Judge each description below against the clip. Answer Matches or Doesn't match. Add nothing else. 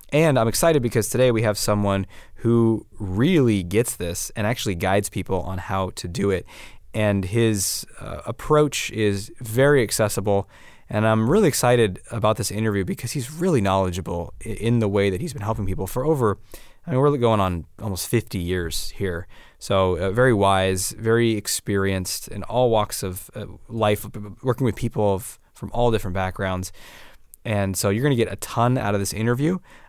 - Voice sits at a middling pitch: Doesn't match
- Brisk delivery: Doesn't match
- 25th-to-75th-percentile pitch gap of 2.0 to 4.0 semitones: Matches